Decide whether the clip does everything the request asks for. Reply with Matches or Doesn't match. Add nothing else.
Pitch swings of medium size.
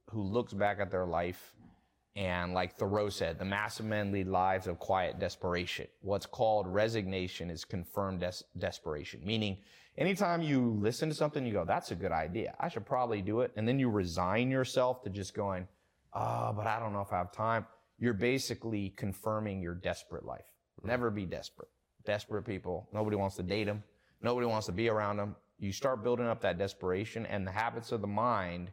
Matches